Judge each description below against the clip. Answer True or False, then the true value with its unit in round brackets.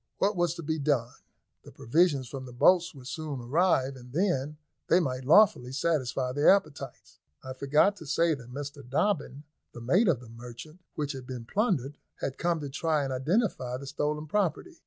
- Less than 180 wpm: False (185 wpm)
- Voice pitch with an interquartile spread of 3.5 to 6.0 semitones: True (4.7 semitones)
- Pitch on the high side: False (145 Hz)